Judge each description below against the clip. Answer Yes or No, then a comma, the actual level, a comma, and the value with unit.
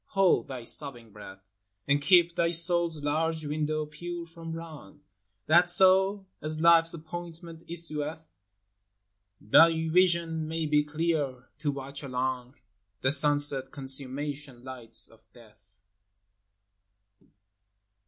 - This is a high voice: No, medium, 150 Hz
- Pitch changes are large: No, average, 3.9 semitones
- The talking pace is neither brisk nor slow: No, slow, 115 wpm